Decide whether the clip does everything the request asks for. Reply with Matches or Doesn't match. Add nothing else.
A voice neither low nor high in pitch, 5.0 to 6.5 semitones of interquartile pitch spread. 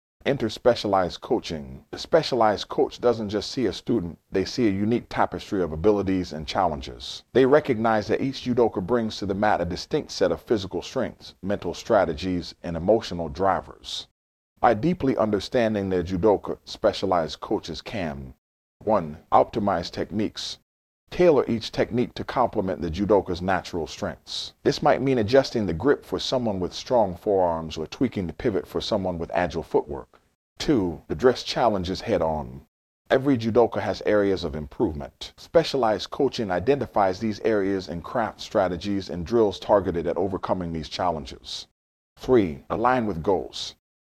Doesn't match